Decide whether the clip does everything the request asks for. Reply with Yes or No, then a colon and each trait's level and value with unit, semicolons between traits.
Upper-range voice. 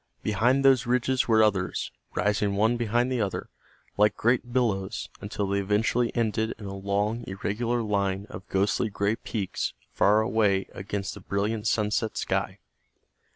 No: low, 105 Hz